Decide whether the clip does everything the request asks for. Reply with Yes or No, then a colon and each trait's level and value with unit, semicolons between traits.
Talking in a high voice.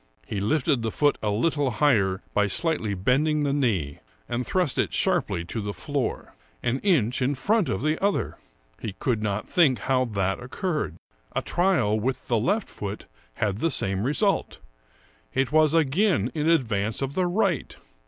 No: low, 130 Hz